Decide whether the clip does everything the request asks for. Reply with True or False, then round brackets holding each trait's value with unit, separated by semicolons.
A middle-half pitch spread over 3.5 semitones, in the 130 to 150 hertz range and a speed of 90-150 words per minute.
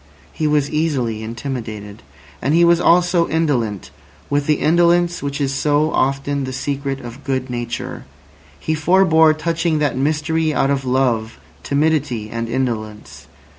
True (4.1 semitones; 140 Hz; 140 wpm)